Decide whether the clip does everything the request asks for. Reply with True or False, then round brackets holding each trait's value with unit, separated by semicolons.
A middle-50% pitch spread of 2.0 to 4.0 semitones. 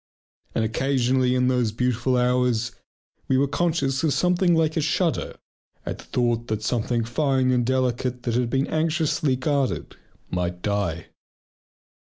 True (3.0 semitones)